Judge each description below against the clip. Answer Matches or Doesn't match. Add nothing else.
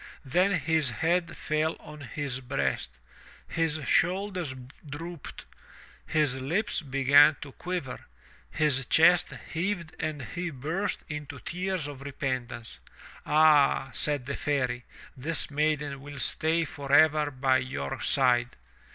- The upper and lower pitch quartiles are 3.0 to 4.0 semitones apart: Matches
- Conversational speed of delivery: Doesn't match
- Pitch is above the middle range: Doesn't match